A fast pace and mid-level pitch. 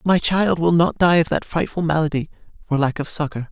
Yes: fast, 220 wpm; medium, 160 Hz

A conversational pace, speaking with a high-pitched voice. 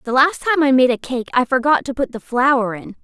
No: fast, 275 wpm; very high, 260 Hz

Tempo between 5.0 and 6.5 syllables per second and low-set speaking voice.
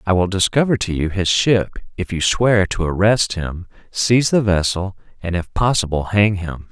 No: 4.8 syllables/s; very low, 95 Hz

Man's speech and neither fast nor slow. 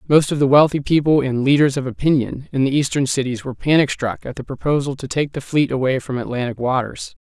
No: male; fast, 225 wpm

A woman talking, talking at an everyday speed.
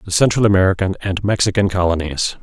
No: male; average, 150 wpm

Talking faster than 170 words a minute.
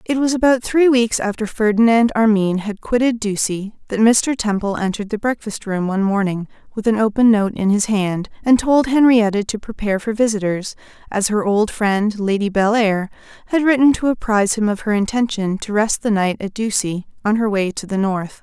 Yes: average, 195 wpm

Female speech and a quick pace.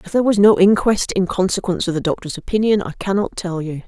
Yes: female; fast, 230 wpm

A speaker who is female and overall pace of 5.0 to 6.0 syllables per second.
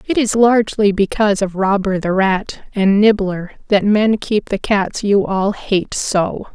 No: female; 4.1 syllables/s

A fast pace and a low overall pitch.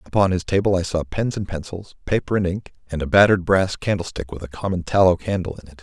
Yes: fast, 235 wpm; very low, 90 Hz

